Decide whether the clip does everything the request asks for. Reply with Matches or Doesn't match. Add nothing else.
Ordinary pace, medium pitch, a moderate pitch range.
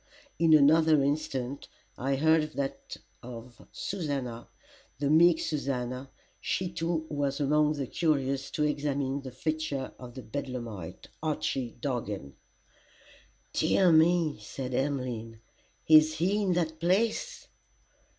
Doesn't match